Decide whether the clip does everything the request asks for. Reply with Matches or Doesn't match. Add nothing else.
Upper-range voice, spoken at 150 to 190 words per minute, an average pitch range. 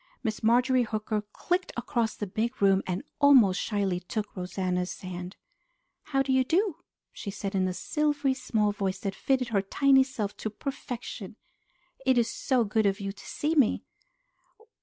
Matches